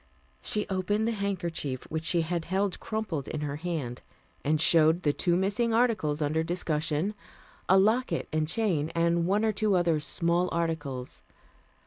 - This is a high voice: No, medium, 170 Hz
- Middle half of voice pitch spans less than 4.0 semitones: No, average, 4.3 semitones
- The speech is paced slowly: No, average, 155 wpm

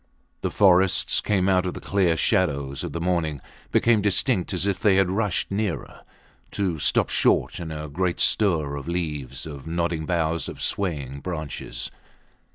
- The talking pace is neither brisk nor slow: Yes, average, 165 wpm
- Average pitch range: Yes, average, 3.8 semitones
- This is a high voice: No, very low, 85 Hz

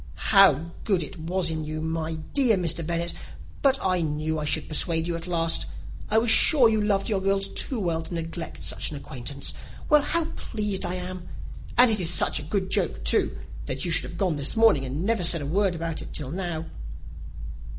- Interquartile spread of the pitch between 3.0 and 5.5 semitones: Yes, average, 3.8 semitones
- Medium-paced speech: No, fast, 210 wpm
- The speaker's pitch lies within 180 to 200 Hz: No, medium, 170 Hz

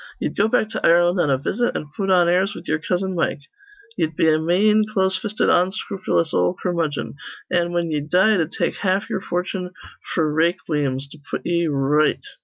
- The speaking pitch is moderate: Yes, medium, 175 Hz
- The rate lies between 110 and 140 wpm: No, average, 200 wpm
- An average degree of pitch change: Yes, average, 3.3 semitones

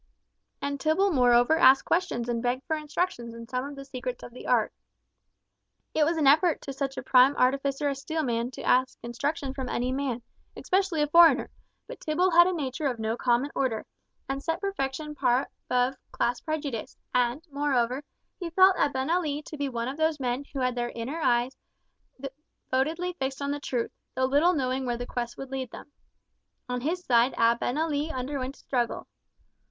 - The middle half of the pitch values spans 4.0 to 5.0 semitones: No, average, 3.6 semitones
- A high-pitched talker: Yes, very high, 270 Hz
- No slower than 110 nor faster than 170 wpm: No, average, 180 wpm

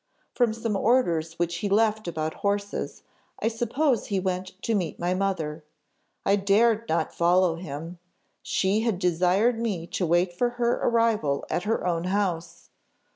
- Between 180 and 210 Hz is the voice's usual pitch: Yes, high, 190 Hz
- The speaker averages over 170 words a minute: No, average, 155 wpm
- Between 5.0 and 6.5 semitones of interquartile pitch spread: No, average, 4.4 semitones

